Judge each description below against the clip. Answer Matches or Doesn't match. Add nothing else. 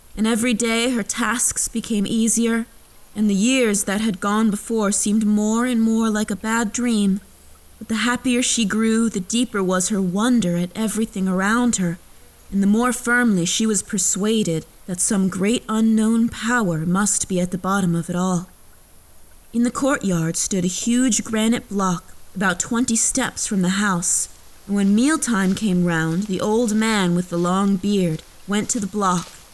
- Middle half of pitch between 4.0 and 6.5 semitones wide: Doesn't match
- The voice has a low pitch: Doesn't match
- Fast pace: Doesn't match